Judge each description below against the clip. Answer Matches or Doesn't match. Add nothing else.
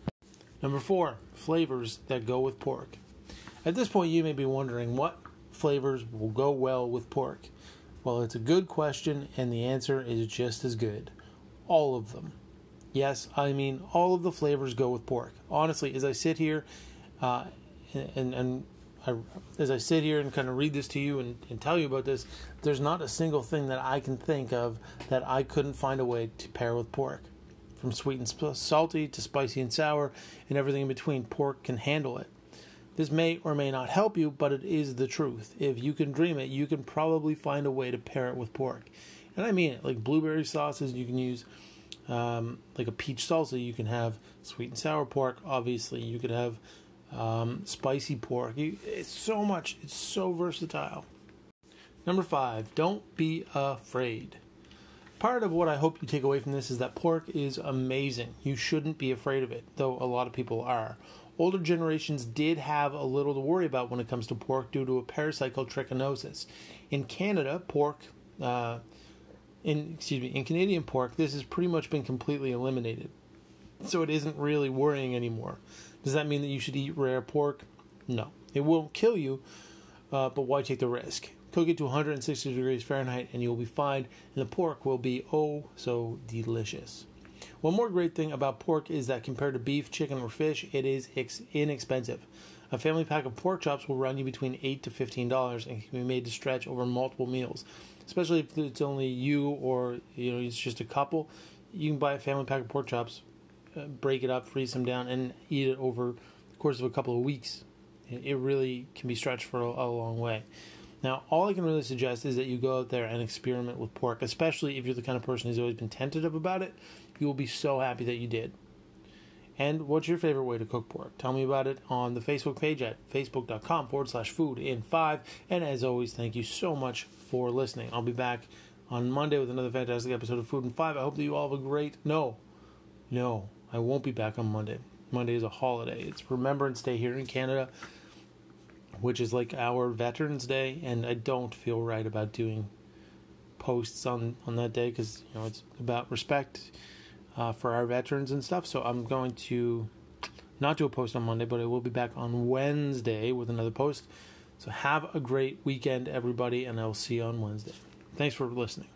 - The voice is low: Matches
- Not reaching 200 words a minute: Doesn't match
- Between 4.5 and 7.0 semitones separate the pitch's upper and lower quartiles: Doesn't match